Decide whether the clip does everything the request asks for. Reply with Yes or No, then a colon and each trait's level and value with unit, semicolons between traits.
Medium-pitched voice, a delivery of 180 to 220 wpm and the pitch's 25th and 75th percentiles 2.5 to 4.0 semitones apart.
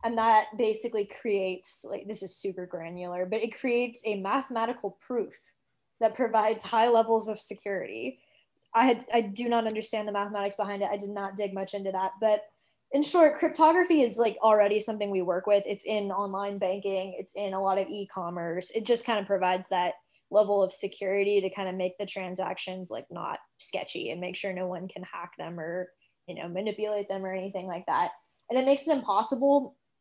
No: high, 205 Hz; average, 200 wpm; average, 3.0 semitones